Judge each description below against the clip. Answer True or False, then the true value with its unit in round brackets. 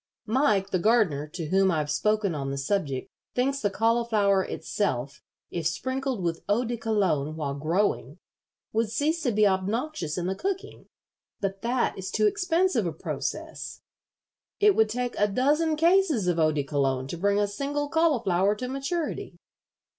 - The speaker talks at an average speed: True (160 wpm)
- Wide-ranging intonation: True (7.2 semitones)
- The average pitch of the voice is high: True (205 Hz)